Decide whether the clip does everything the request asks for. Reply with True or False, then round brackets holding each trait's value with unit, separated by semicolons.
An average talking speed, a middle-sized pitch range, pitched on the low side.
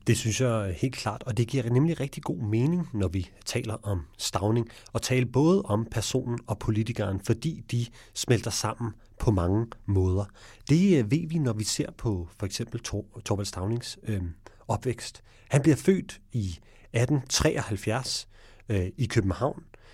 True (160 wpm; 3.7 semitones; 115 Hz)